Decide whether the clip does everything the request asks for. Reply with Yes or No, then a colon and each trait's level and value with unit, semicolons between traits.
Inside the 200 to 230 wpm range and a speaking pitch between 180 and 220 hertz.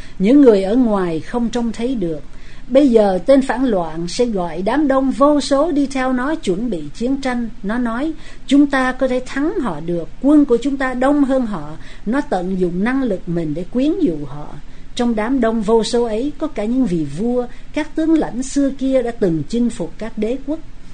No: average, 215 wpm; high, 245 Hz